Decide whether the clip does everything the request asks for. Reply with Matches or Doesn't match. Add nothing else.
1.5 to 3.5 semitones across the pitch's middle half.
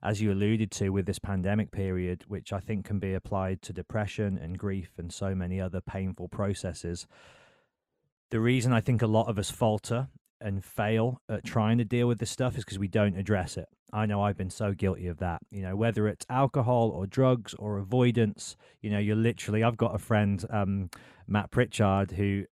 Matches